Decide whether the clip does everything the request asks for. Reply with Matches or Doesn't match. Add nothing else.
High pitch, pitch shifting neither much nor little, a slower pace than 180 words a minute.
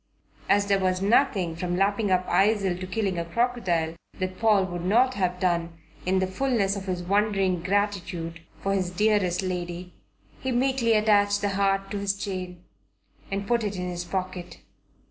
Doesn't match